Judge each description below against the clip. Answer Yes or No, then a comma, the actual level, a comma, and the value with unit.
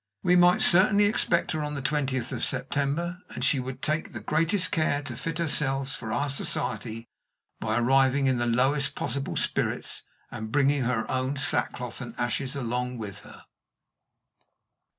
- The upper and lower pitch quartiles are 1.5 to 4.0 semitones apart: Yes, average, 3.6 semitones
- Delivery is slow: No, average, 160 wpm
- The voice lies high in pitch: No, low, 135 Hz